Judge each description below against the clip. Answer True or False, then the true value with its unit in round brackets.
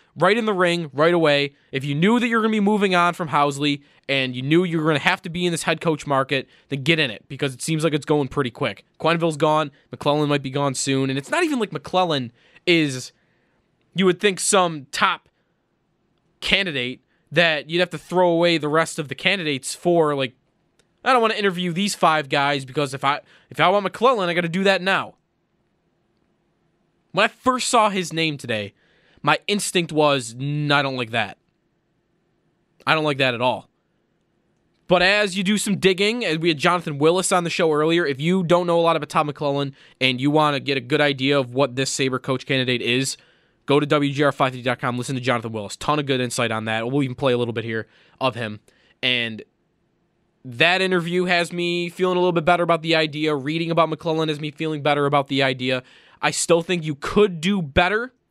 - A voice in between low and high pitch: True (155 Hz)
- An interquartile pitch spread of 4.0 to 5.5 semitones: True (4.3 semitones)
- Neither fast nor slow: False (215 wpm)